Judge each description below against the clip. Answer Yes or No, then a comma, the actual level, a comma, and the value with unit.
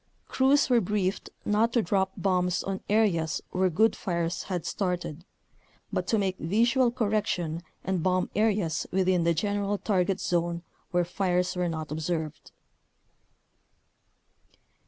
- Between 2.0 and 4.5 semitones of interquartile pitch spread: Yes, average, 3.1 semitones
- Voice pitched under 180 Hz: No, medium, 185 Hz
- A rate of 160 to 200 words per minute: No, slow, 135 wpm